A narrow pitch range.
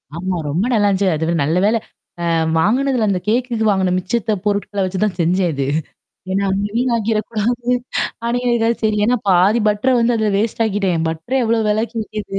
No: average, 3.7 semitones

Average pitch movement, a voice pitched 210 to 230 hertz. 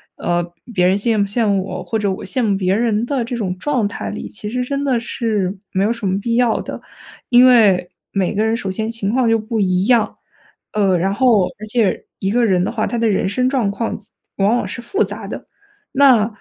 Yes: average, 3.3 semitones; high, 215 Hz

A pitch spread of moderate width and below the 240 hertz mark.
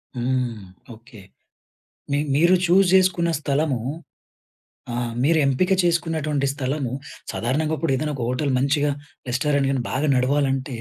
Yes: average, 3.5 semitones; medium, 140 Hz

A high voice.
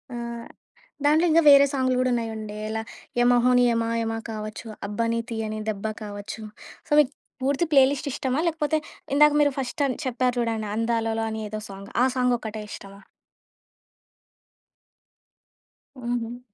Yes: high, 235 Hz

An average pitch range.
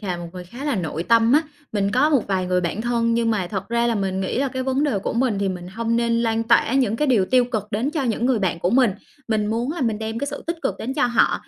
Yes: average, 4.3 semitones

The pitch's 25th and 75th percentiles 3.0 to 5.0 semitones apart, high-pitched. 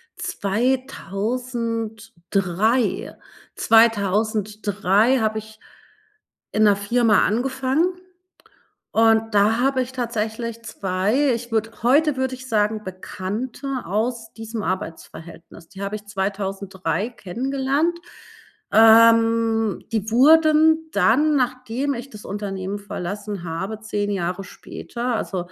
Yes: average, 3.6 semitones; high, 225 Hz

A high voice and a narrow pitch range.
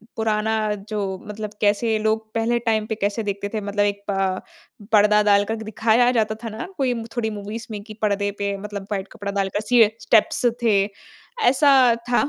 Yes: high, 215 Hz; narrow, 1.6 semitones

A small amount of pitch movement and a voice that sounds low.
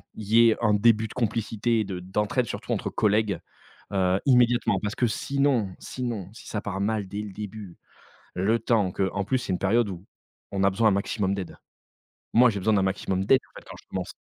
No: average, 3.0 semitones; low, 105 Hz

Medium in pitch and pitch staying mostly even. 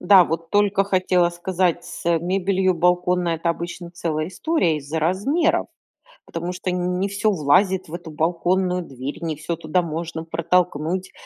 Yes: medium, 175 Hz; narrow, 2.1 semitones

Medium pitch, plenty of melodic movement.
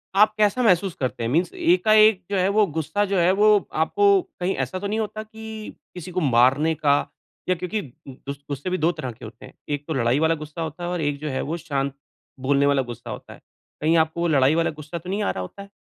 Yes: medium, 170 Hz; wide, 5.9 semitones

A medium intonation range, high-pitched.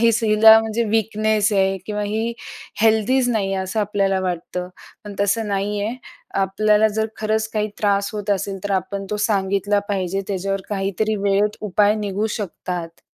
No: narrow, 1.8 semitones; high, 205 Hz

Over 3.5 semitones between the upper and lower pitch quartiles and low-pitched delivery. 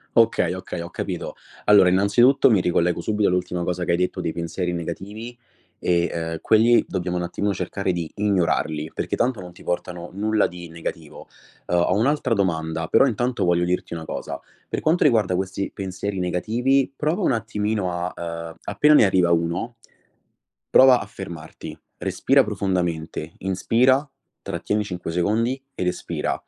Yes: average, 4.1 semitones; very low, 95 Hz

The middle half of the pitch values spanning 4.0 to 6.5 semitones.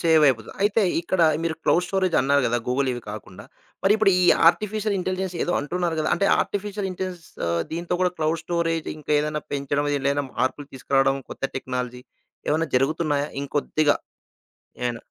Yes: average, 4.6 semitones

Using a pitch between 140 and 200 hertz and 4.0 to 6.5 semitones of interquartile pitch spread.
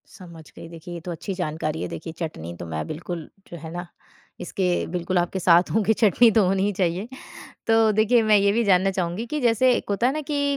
Yes: medium, 185 Hz; average, 4.4 semitones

